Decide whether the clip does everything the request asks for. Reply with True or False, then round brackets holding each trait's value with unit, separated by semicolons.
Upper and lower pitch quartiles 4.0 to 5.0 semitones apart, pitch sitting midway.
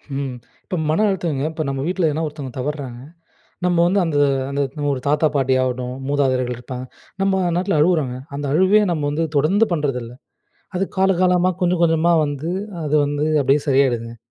True (4.5 semitones; 150 Hz)